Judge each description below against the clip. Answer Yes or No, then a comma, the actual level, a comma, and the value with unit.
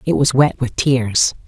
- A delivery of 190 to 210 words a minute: Yes, fast, 205 wpm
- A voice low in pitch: Yes, low, 115 Hz